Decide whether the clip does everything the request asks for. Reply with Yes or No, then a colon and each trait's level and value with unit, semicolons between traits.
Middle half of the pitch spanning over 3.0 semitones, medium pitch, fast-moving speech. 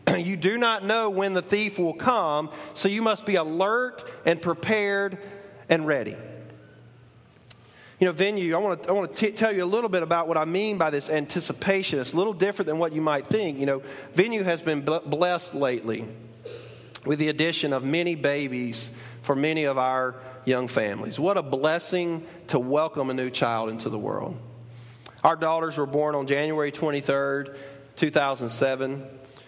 No: average, 5.1 semitones; medium, 155 Hz; average, 175 wpm